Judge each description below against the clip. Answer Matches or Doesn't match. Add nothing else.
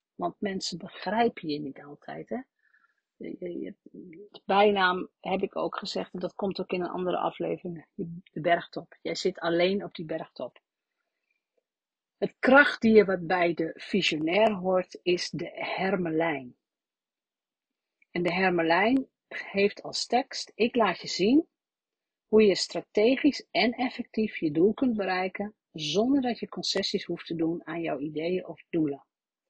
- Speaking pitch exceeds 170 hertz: Matches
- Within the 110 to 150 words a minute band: Matches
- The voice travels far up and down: Doesn't match